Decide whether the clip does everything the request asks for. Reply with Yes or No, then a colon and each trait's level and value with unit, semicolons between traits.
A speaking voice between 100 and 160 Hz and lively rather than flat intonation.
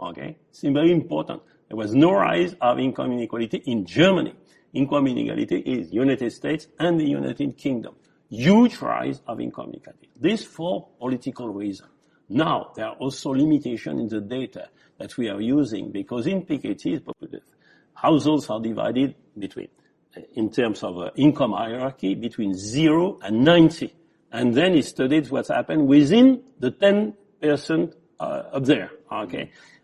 Yes: medium, 140 Hz; wide, 6.0 semitones